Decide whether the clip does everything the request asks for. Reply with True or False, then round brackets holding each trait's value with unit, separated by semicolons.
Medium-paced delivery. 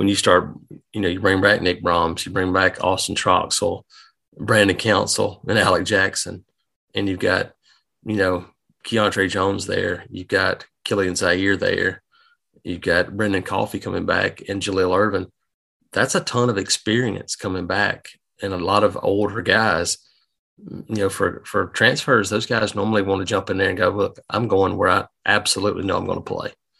True (180 wpm)